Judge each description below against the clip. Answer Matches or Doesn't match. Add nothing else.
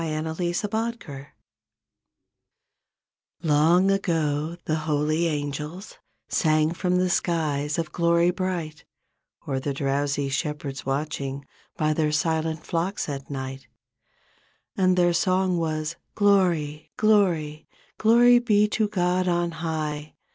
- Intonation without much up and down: Doesn't match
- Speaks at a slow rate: Matches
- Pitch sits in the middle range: Matches